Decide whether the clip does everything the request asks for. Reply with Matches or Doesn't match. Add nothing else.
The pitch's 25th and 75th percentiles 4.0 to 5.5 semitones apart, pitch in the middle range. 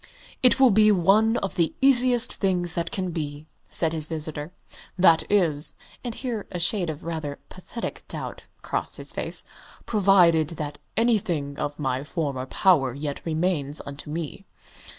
Matches